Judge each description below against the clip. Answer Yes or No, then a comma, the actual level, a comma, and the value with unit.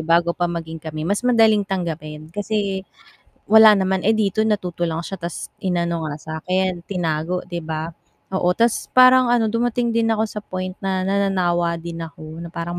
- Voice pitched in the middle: Yes, medium, 180 Hz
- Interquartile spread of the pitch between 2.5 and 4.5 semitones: Yes, average, 3.8 semitones